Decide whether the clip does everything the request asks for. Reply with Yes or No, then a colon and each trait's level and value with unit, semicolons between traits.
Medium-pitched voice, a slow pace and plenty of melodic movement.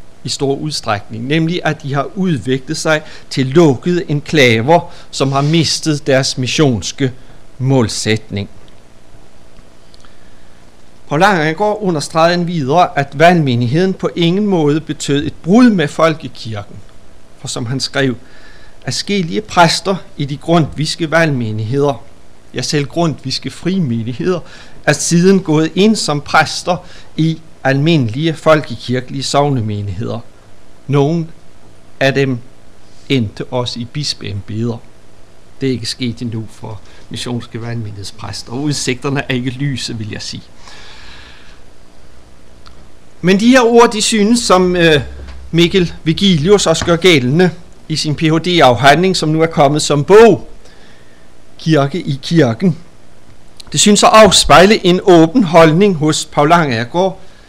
Yes: medium, 145 Hz; slow, 125 wpm; wide, 6.2 semitones